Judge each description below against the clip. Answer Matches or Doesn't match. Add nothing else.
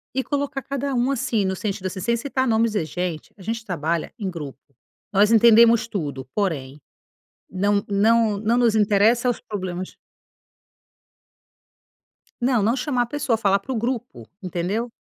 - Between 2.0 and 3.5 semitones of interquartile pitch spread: Doesn't match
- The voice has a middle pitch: Doesn't match